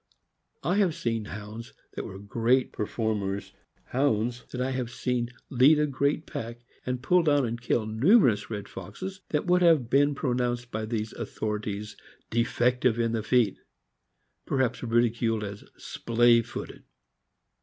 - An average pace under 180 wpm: Yes, average, 150 wpm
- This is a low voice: Yes, low, 120 Hz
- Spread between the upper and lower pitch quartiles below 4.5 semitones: Yes, average, 3.2 semitones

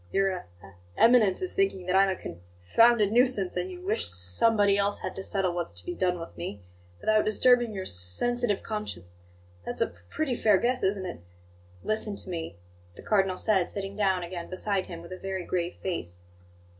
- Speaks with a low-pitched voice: No, high, 195 Hz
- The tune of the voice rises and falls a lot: No, average, 3.5 semitones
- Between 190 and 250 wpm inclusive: Yes, average, 200 wpm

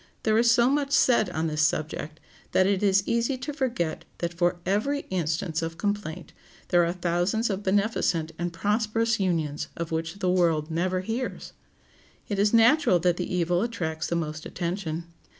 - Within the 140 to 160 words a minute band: No, average, 170 wpm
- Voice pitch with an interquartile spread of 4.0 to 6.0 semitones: Yes, average, 4.7 semitones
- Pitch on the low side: No, medium, 180 Hz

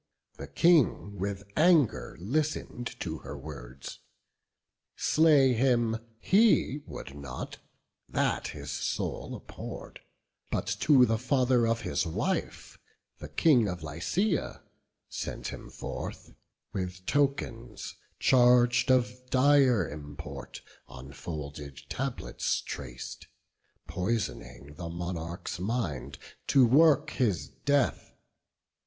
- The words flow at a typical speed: No, slow, 100 wpm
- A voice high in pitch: No, low, 115 Hz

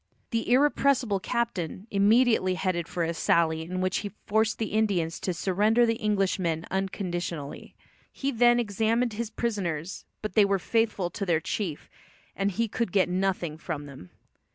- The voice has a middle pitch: No, high, 195 Hz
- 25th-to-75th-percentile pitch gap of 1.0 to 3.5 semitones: No, average, 4.4 semitones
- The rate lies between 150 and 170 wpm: Yes, average, 155 wpm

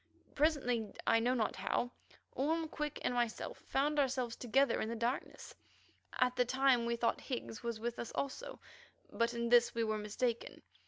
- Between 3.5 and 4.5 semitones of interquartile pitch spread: No, narrow, 2.6 semitones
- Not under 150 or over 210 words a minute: Yes, average, 170 wpm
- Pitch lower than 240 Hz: No, high, 245 Hz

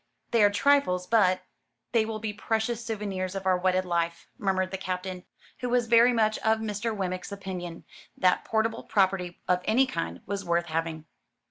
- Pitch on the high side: Yes, high, 195 Hz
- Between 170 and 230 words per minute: Yes, average, 175 wpm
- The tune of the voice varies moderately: Yes, average, 3.4 semitones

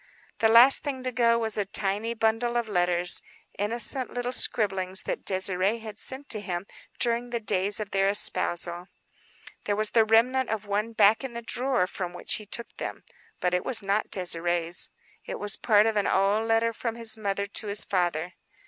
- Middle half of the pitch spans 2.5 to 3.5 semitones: Yes, average, 3.2 semitones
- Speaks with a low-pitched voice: No, high, 215 Hz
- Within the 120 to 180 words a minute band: No, average, 190 wpm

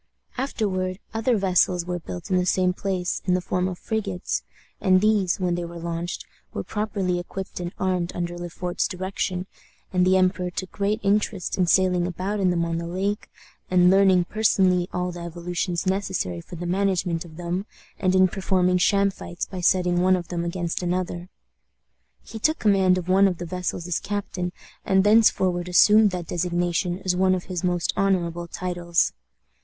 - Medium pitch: Yes, medium, 180 Hz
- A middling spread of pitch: No, narrow, 1.5 semitones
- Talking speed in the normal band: Yes, average, 180 wpm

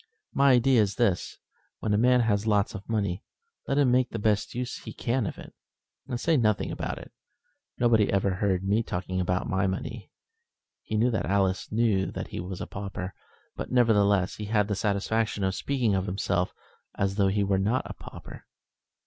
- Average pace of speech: Yes, average, 190 wpm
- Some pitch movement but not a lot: Yes, average, 3.1 semitones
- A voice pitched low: Yes, low, 105 Hz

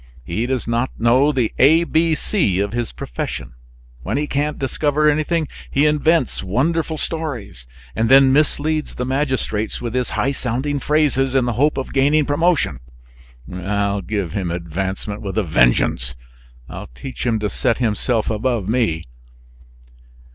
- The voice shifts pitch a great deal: Yes, wide, 6.1 semitones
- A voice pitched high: No, low, 125 Hz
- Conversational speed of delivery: Yes, average, 150 wpm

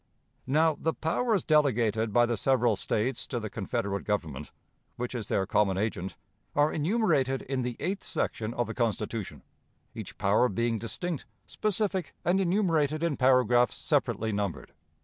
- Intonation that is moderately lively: No, wide, 6.2 semitones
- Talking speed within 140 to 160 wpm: Yes, average, 150 wpm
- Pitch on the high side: No, low, 125 Hz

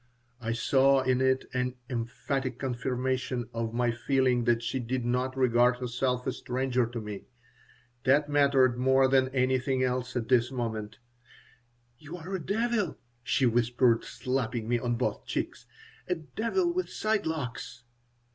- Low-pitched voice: Yes, low, 130 Hz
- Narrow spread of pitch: Yes, narrow, 1.9 semitones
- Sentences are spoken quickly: No, average, 145 wpm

